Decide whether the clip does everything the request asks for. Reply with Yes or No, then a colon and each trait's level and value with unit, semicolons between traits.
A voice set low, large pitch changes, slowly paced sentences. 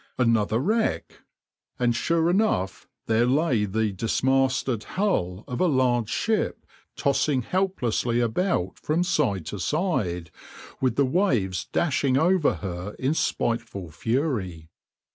Yes: low, 125 Hz; wide, 7.3 semitones; slow, 120 wpm